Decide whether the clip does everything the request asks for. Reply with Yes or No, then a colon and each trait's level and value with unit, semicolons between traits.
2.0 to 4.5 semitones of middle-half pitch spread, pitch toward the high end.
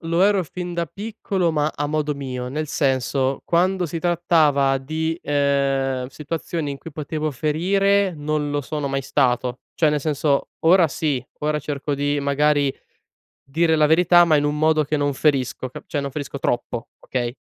No: average, 2.8 semitones; medium, 150 Hz